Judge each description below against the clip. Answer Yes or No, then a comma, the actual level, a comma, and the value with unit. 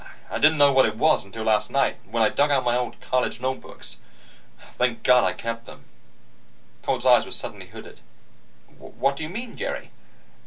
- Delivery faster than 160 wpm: Yes, average, 185 wpm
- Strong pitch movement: No, average, 3.6 semitones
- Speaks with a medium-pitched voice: No, low, 125 Hz